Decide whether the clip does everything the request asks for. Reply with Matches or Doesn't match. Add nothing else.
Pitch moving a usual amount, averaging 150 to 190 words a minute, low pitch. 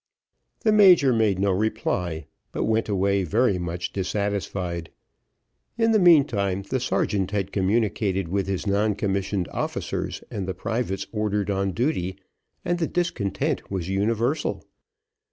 Doesn't match